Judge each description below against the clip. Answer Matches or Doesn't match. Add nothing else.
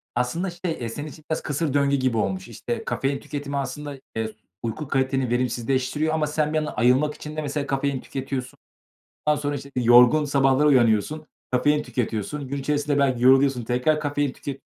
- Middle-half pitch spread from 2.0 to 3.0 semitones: Matches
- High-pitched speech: Doesn't match